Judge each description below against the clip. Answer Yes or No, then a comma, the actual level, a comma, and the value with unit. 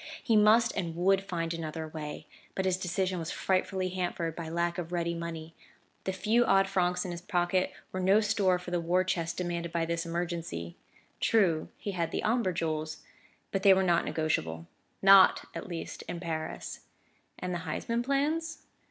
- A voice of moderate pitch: Yes, medium, 175 Hz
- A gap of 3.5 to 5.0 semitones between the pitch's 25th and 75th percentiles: No, narrow, 2.4 semitones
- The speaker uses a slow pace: No, average, 180 wpm